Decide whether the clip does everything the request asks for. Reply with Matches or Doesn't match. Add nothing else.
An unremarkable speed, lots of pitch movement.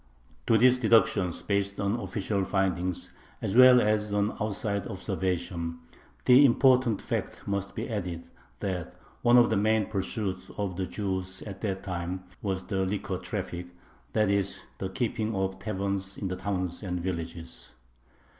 Doesn't match